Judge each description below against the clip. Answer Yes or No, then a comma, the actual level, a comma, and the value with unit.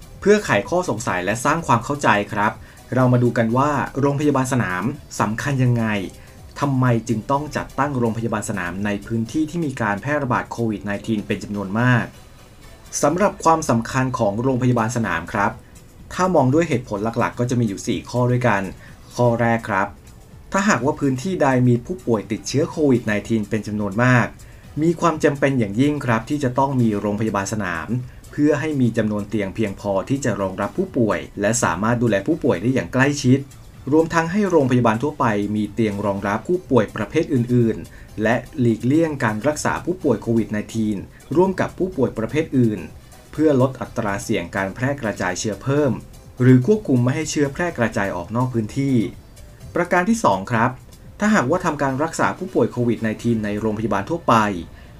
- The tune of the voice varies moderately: Yes, average, 4.3 semitones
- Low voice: Yes, low, 120 Hz